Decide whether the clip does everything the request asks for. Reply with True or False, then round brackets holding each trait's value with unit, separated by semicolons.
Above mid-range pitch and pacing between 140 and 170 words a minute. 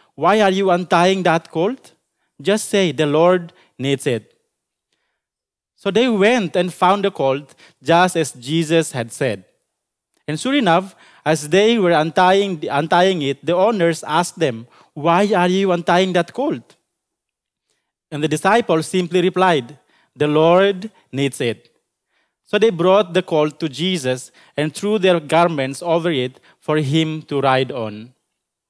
False (170 Hz; 145 wpm)